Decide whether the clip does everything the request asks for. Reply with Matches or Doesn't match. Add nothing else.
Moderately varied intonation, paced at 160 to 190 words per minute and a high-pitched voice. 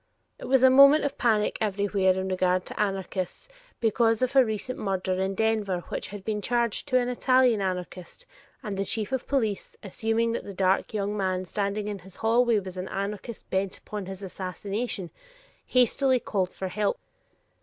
Matches